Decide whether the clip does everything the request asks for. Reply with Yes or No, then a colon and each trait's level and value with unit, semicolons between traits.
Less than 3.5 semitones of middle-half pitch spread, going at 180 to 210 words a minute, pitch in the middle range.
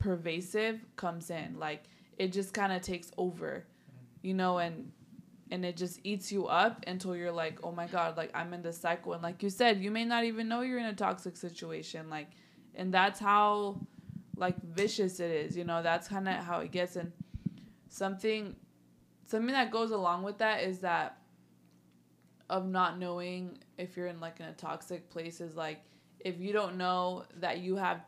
Yes: average, 2.8 semitones; average, 190 wpm; medium, 180 Hz